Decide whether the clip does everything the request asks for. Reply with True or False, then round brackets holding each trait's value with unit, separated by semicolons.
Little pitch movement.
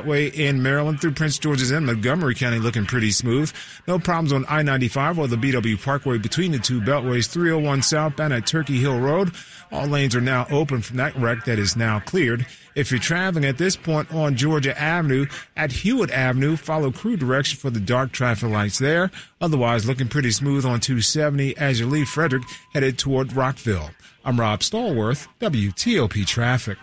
False (3.8 semitones)